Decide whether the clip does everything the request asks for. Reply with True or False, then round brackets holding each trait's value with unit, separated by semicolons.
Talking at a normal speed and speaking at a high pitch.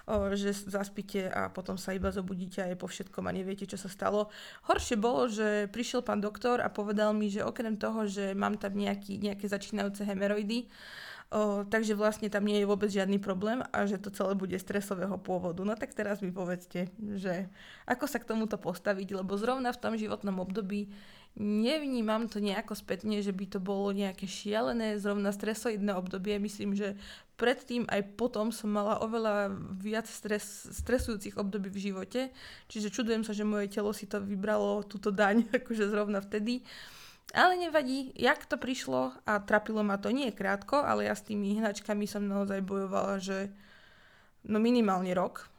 False (170 wpm; 205 Hz)